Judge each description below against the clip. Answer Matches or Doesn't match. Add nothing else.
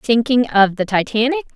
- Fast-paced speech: Doesn't match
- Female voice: Matches